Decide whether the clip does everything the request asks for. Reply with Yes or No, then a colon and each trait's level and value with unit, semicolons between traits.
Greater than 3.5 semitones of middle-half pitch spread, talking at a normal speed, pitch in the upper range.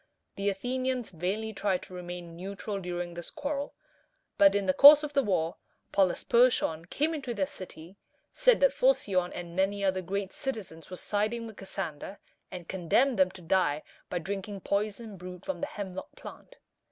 Yes: average, 4.1 semitones; average, 165 wpm; high, 195 Hz